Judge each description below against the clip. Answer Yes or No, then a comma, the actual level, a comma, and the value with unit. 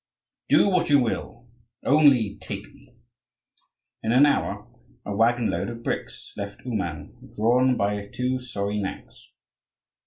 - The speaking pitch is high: No, low, 115 Hz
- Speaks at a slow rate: Yes, slow, 130 wpm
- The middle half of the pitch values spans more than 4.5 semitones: No, average, 3.9 semitones